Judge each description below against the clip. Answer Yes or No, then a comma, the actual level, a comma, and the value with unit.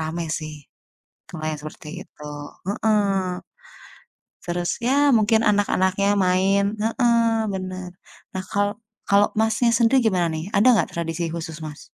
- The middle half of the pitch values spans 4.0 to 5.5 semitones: Yes, average, 4.7 semitones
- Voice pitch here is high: Yes, high, 195 Hz